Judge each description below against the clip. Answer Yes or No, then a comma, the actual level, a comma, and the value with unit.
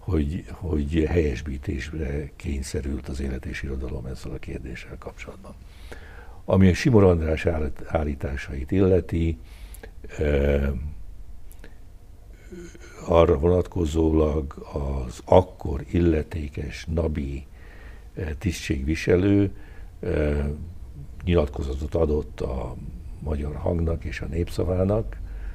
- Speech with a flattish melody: No, average, 3.2 semitones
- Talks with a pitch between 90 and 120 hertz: No, very low, 80 Hz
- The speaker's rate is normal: No, slow, 80 wpm